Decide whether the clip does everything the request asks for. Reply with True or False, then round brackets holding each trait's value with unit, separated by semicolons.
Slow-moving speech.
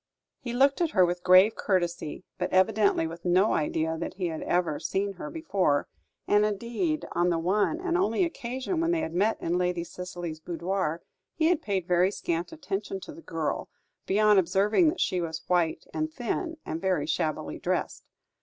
False (180 wpm)